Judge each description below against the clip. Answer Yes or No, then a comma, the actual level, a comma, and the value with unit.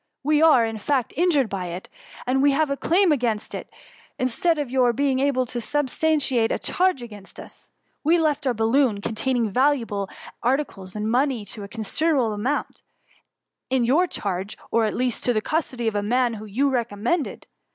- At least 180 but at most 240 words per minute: Yes, average, 185 wpm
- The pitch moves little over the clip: No, average, 4.6 semitones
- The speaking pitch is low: No, very high, 250 Hz